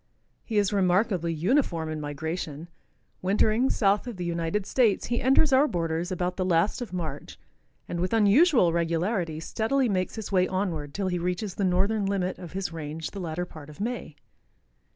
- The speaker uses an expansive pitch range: No, average, 4.0 semitones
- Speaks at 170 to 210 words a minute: Yes, average, 175 wpm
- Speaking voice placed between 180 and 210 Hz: Yes, medium, 185 Hz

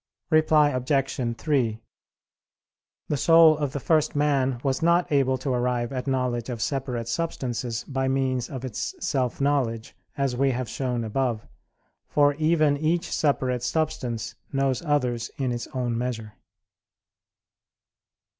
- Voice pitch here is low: Yes, low, 130 Hz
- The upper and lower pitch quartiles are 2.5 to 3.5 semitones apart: Yes, average, 2.9 semitones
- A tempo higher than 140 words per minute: No, slow, 135 wpm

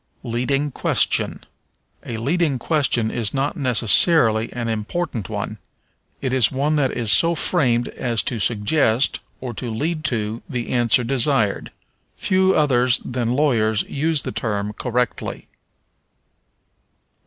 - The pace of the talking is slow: Yes, slow, 120 wpm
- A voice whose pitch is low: Yes, low, 125 Hz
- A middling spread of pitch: Yes, average, 4.1 semitones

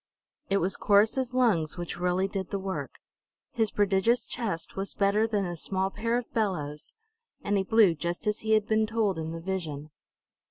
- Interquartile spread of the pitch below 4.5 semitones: Yes, average, 3.6 semitones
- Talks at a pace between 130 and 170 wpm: No, average, 185 wpm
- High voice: Yes, high, 195 Hz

